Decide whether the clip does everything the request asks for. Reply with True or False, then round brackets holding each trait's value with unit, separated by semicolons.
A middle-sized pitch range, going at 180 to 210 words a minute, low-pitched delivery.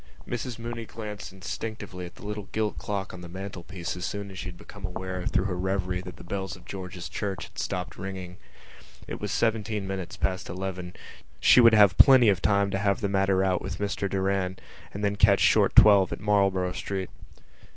False (1.9 semitones; 200 wpm; 95 Hz)